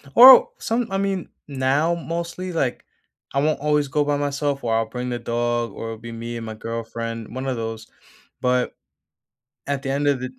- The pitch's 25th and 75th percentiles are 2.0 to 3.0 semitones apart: No, average, 4.2 semitones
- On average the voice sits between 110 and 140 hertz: Yes, low, 135 Hz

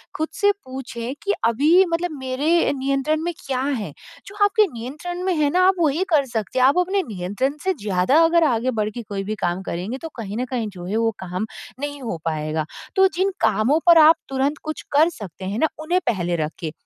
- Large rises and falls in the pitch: Yes, wide, 7.3 semitones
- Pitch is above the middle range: Yes, very high, 265 Hz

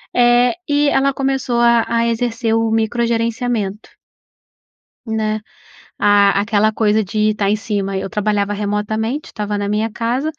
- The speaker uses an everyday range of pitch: No, narrow, 2.3 semitones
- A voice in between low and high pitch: No, high, 220 Hz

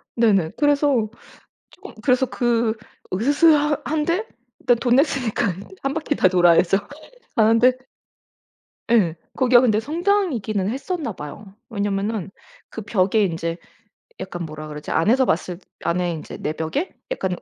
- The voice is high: Yes, high, 225 Hz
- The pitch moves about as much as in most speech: No, wide, 6.9 semitones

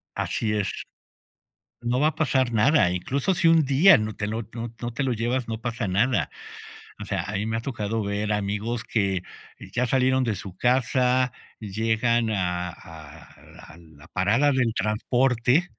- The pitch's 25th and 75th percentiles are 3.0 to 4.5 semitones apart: Yes, average, 3.8 semitones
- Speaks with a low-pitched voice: Yes, low, 115 Hz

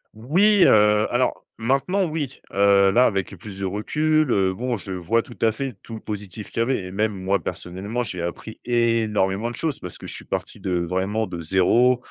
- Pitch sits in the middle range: No, low, 110 Hz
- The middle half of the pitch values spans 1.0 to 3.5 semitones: No, average, 4.3 semitones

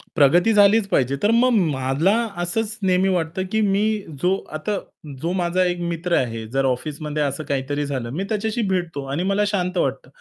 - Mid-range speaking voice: Yes, medium, 175 Hz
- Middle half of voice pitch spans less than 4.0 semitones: No, wide, 5.5 semitones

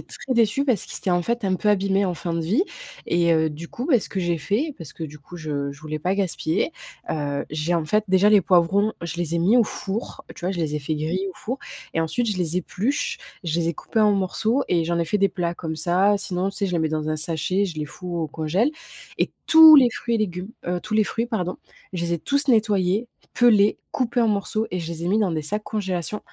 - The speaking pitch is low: No, medium, 185 Hz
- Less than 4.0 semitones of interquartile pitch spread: No, average, 4.3 semitones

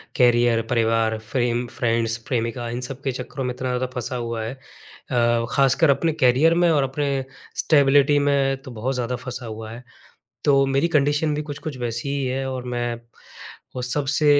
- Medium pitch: No, low, 130 Hz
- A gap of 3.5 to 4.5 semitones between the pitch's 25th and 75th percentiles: No, average, 2.8 semitones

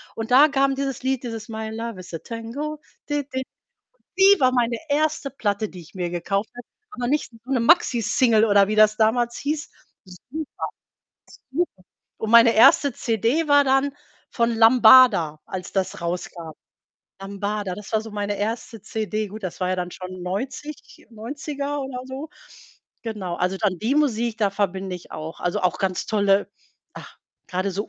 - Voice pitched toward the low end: No, high, 225 Hz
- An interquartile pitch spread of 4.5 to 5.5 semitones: Yes, average, 5.0 semitones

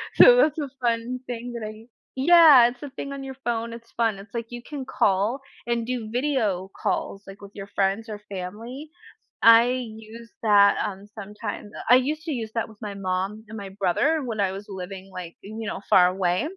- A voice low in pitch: No, high, 225 Hz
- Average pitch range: Yes, average, 3.8 semitones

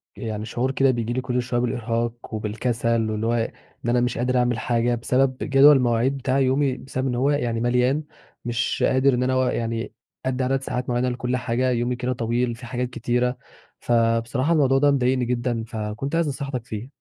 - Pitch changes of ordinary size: No, narrow, 1.8 semitones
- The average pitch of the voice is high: No, low, 125 Hz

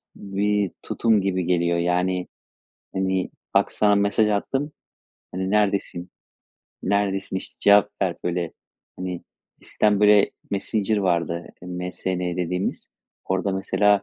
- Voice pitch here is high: No, very low, 95 Hz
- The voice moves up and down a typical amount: No, narrow, 2.3 semitones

